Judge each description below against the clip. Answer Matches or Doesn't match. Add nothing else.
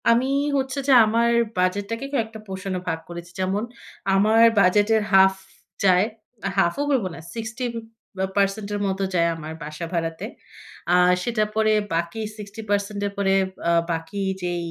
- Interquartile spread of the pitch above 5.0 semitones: Doesn't match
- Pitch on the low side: Doesn't match